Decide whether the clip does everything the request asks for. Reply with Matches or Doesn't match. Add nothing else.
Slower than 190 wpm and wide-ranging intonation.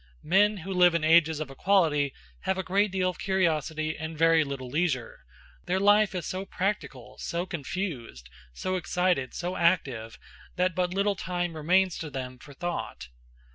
Doesn't match